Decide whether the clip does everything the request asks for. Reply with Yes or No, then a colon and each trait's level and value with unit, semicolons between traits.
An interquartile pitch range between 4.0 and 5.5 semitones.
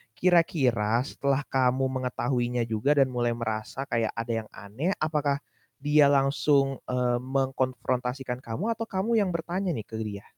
No: average, 3.4 semitones